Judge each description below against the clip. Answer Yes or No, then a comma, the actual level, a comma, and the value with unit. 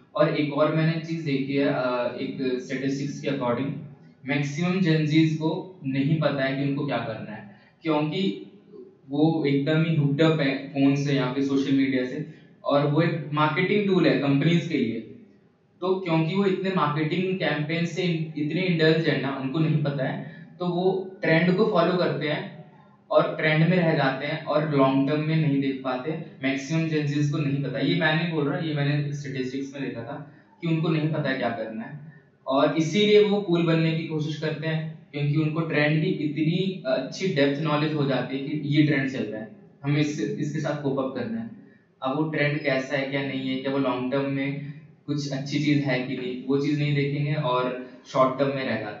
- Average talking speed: No, fast, 200 wpm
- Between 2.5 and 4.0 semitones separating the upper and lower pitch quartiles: Yes, average, 2.8 semitones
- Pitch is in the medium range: Yes, medium, 150 Hz